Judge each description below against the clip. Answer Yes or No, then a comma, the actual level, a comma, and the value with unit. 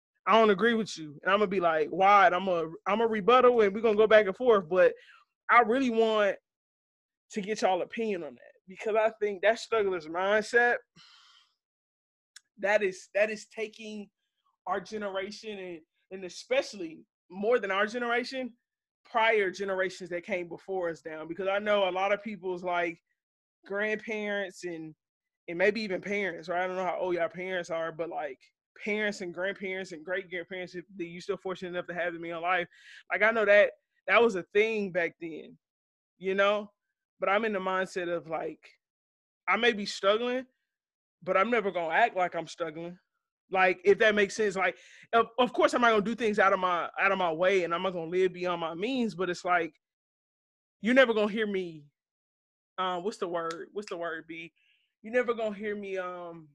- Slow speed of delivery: No, average, 195 wpm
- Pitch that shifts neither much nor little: Yes, average, 3.7 semitones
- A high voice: Yes, high, 195 Hz